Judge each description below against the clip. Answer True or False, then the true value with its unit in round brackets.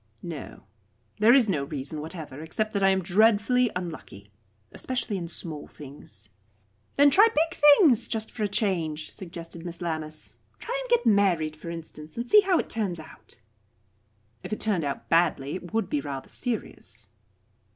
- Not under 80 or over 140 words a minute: False (165 wpm)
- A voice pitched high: False (180 Hz)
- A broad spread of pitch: True (6.4 semitones)